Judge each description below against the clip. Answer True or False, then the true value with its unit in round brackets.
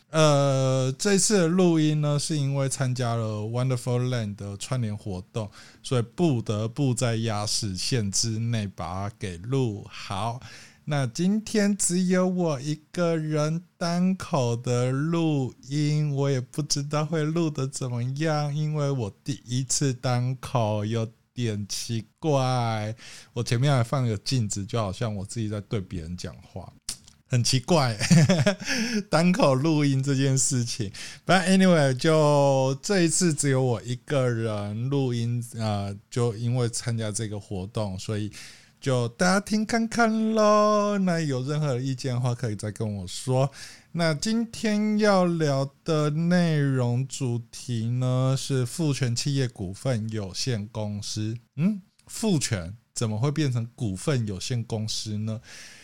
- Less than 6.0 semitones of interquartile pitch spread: True (5.2 semitones)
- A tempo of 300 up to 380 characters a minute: False (225 characters per minute)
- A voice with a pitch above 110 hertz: True (130 Hz)